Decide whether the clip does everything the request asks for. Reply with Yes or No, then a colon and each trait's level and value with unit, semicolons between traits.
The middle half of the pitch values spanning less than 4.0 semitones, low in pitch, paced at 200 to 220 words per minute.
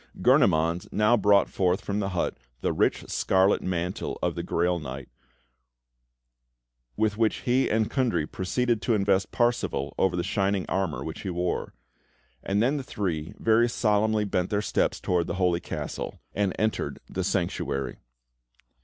No: average, 3.6 semitones; very low, 95 Hz; average, 155 wpm